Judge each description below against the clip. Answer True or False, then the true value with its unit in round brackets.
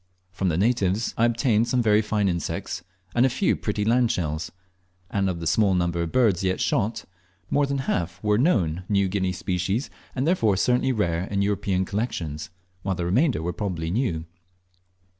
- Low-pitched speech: True (100 Hz)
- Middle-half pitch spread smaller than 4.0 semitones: False (4.7 semitones)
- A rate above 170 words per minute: True (180 wpm)